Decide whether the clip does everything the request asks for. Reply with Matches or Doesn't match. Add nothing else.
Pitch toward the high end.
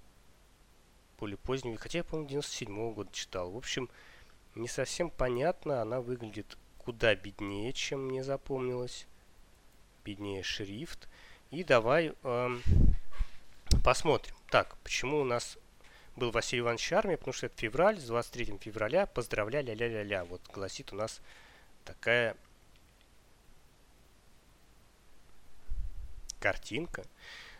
Doesn't match